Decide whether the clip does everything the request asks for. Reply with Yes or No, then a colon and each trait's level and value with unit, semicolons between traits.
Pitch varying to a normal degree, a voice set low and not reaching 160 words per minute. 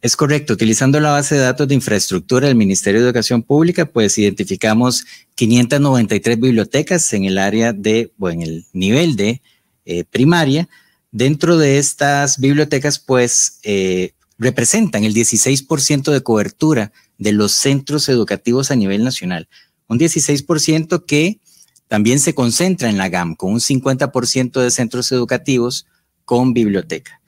Yes: average, 4.8 semitones; low, 125 Hz; average, 140 wpm